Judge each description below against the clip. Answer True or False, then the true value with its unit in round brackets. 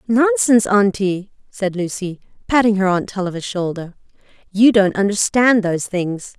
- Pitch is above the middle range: True (200 Hz)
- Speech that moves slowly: True (130 wpm)